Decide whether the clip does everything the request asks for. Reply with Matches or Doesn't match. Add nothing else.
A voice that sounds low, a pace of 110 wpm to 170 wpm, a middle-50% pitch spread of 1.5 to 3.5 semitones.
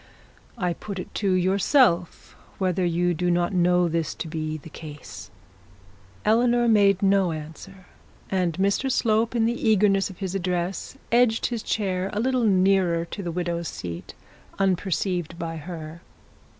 Doesn't match